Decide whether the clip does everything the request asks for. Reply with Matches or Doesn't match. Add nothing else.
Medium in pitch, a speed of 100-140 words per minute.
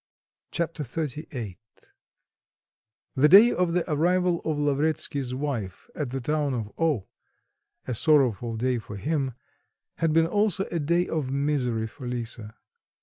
Matches